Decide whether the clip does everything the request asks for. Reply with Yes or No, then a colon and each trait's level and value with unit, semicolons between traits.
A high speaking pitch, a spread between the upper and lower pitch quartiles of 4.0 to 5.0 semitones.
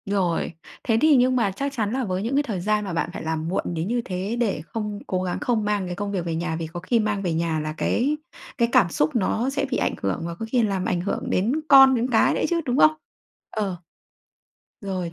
No: high, 205 Hz; wide, 5.4 semitones